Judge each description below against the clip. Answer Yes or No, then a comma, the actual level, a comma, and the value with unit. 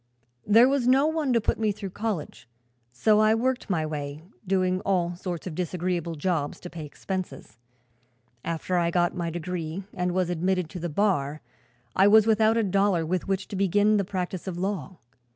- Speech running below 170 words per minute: No, average, 185 wpm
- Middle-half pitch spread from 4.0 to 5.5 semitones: No, average, 3.3 semitones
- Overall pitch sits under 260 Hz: Yes, medium, 185 Hz